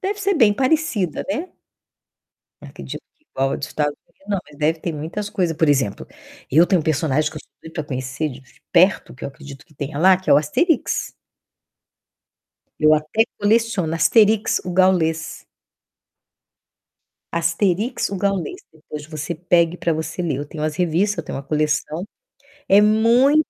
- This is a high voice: No, medium, 170 Hz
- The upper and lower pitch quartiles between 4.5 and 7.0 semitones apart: Yes, average, 5.0 semitones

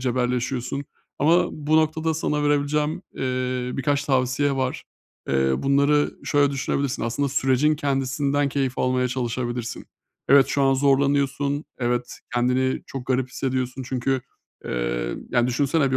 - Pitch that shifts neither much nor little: No, narrow, 2.1 semitones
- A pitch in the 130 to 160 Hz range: Yes, low, 135 Hz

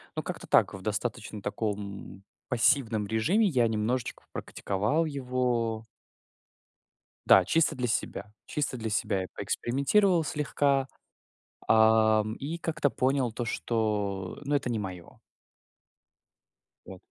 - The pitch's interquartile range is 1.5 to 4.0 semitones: No, average, 4.5 semitones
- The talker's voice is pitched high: No, low, 115 Hz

